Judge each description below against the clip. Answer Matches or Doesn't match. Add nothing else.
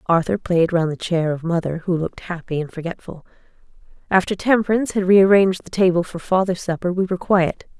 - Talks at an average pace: Matches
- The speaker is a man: Doesn't match